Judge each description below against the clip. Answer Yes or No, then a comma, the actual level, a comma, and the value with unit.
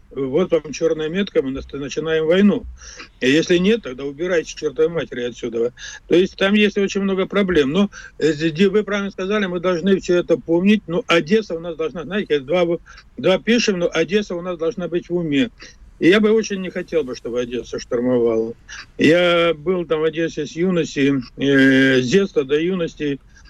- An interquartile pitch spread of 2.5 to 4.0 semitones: No, average, 5.1 semitones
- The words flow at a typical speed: No, fast, 175 wpm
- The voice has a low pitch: No, medium, 170 Hz